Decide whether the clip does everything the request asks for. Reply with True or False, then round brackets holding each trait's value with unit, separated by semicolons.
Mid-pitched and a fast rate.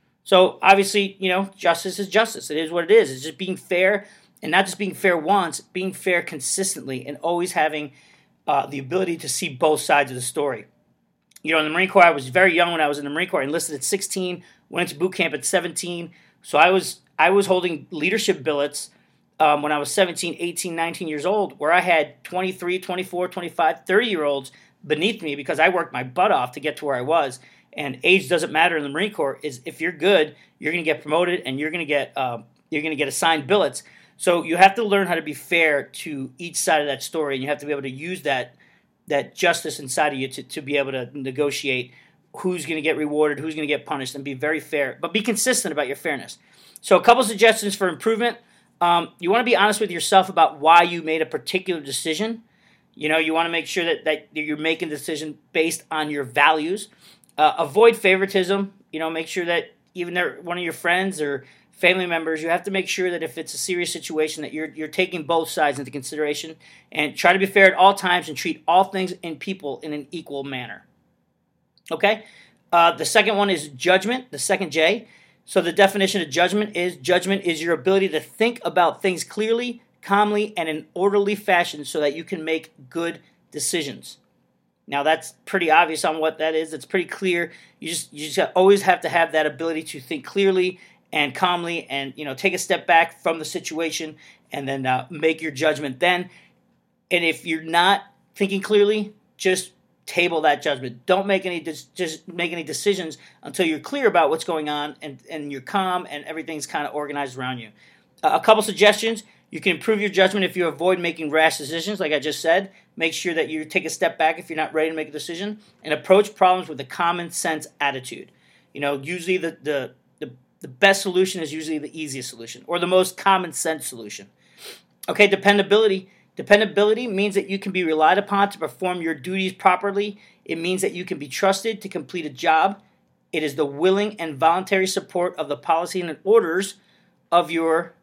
True (170 Hz; 220 wpm)